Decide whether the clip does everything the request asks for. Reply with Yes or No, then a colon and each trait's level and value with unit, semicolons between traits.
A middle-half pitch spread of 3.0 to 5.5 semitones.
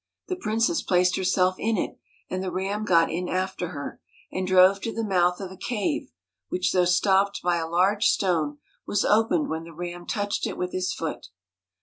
No: narrow, 2.4 semitones